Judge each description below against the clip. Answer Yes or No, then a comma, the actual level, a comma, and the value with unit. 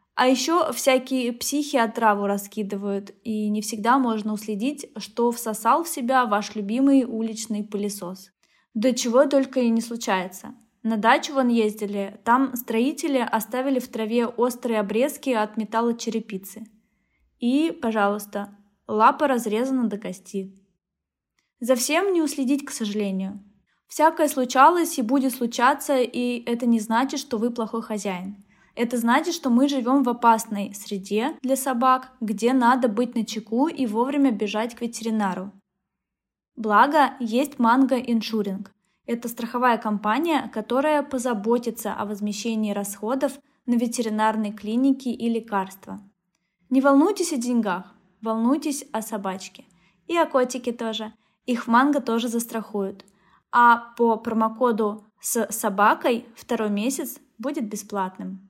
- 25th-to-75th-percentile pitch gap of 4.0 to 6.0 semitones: No, average, 3.5 semitones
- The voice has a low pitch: No, high, 230 Hz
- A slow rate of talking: No, average, 130 wpm